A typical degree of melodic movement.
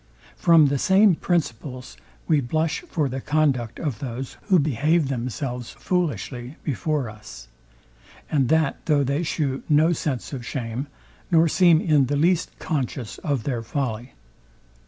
Yes: average, 4.2 semitones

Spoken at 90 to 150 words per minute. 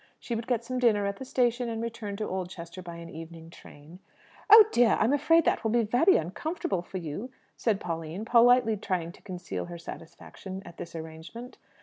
No: average, 195 wpm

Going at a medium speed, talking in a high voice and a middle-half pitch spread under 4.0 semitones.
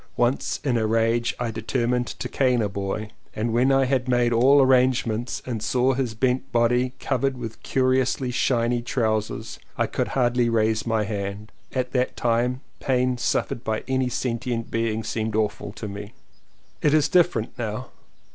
No: average, 160 wpm; low, 120 Hz; narrow, 2.4 semitones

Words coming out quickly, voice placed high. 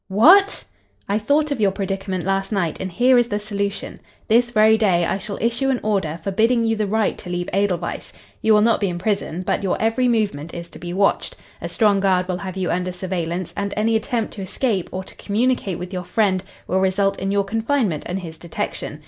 Yes: fast, 215 wpm; high, 200 Hz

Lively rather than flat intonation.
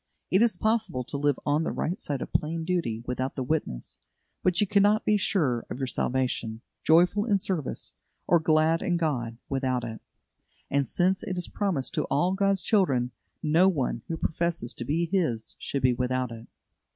Yes: wide, 6.2 semitones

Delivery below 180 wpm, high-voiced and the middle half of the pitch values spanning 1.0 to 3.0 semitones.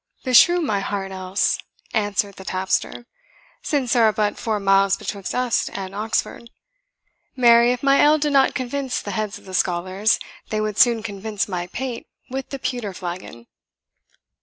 No: average, 160 wpm; high, 215 Hz; average, 4.2 semitones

